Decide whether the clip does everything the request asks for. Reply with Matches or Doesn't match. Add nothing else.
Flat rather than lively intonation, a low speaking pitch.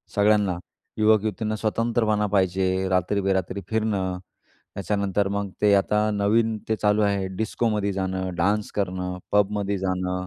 Matches